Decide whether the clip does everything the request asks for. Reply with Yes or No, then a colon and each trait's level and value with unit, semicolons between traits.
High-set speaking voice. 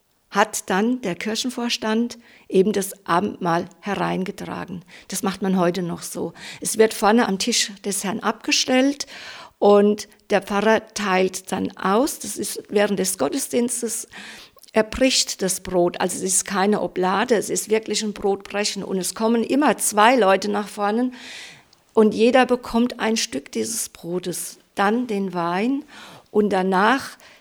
Yes: high, 210 Hz